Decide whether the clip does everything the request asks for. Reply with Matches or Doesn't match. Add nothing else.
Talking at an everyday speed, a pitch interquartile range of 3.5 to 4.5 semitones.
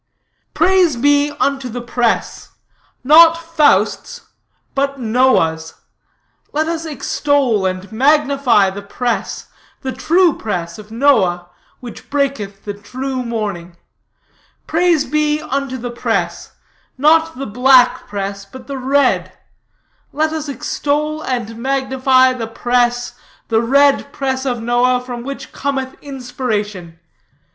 Doesn't match